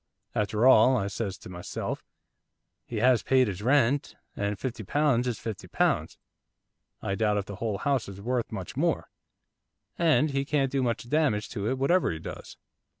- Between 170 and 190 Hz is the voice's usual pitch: No, low, 120 Hz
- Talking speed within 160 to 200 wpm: Yes, average, 175 wpm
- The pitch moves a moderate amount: Yes, average, 4.7 semitones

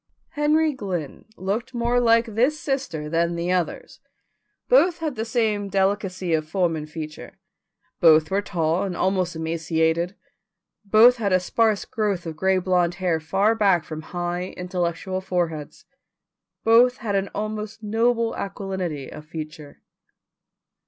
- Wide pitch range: No, average, 4.8 semitones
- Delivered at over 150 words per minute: No, average, 140 wpm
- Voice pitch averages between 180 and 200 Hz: Yes, high, 190 Hz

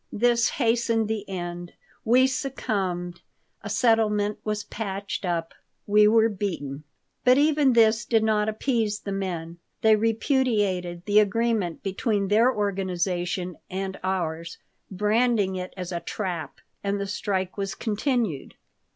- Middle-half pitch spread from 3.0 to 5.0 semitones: Yes, average, 3.5 semitones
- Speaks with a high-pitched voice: Yes, high, 205 Hz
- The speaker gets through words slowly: Yes, slow, 130 wpm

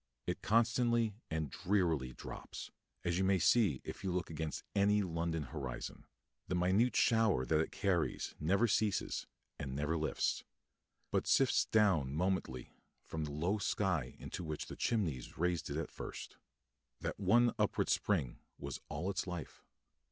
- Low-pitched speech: Yes, very low, 90 Hz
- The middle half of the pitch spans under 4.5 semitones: No, average, 4.9 semitones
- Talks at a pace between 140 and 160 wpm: Yes, average, 150 wpm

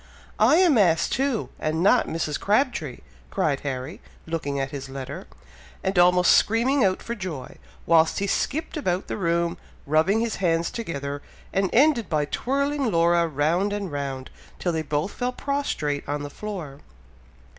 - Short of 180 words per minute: Yes, average, 155 wpm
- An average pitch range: No, wide, 6.9 semitones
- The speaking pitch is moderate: Yes, medium, 170 Hz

